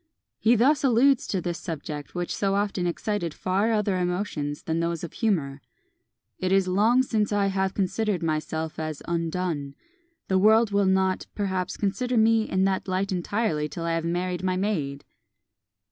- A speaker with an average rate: Yes, average, 165 wpm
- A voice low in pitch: No, medium, 185 Hz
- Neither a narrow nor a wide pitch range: Yes, average, 3.7 semitones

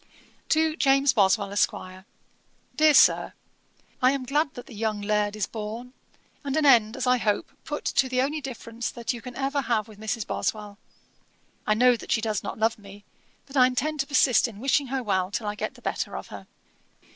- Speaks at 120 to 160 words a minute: No, fast, 205 wpm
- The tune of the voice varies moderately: Yes, average, 4.3 semitones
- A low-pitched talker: No, high, 240 Hz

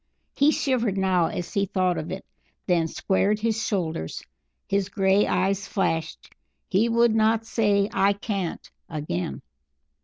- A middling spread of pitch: Yes, average, 3.3 semitones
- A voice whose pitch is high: Yes, high, 195 Hz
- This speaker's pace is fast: No, average, 140 wpm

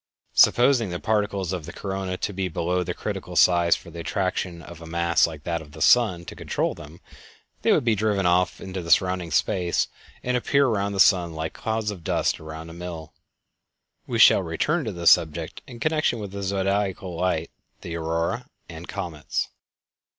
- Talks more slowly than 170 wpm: No, average, 190 wpm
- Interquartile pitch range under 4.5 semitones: Yes, average, 3.2 semitones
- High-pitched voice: No, very low, 90 Hz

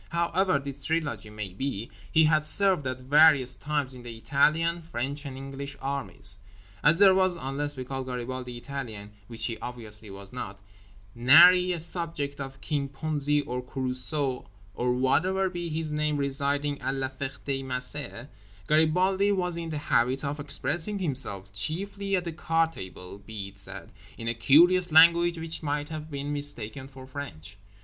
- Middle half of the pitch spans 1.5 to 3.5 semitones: No, average, 4.1 semitones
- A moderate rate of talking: Yes, average, 160 wpm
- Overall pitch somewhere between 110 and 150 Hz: Yes, medium, 140 Hz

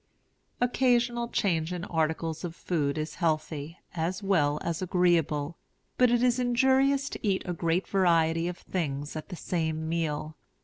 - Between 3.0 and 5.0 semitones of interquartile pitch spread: Yes, average, 4.0 semitones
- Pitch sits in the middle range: Yes, medium, 170 Hz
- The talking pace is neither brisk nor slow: Yes, average, 150 wpm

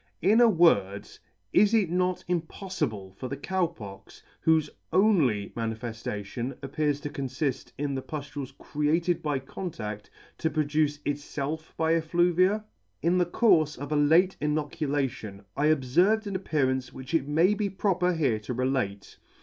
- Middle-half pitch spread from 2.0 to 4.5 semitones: No, average, 5.1 semitones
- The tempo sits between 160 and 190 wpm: No, average, 150 wpm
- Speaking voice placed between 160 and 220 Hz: No, medium, 150 Hz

